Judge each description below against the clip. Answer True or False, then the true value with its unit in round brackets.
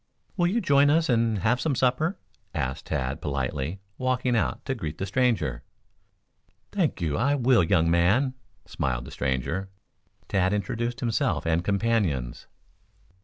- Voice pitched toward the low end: True (105 Hz)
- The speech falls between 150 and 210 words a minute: False (140 wpm)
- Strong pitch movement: True (8.0 semitones)